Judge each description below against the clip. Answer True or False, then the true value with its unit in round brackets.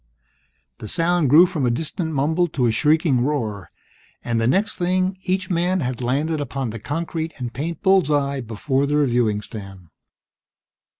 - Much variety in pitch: True (5.7 semitones)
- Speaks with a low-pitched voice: False (145 Hz)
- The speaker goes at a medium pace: True (165 wpm)